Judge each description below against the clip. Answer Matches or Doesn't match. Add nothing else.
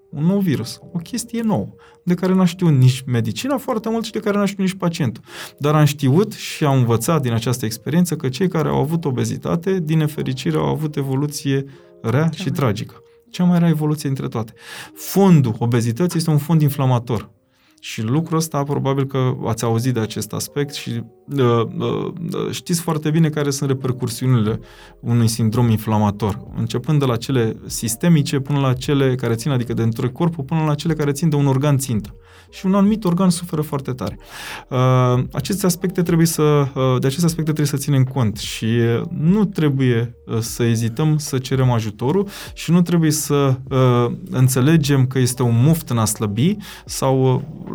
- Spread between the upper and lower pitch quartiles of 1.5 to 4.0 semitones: Doesn't match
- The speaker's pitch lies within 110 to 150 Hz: Matches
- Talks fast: Matches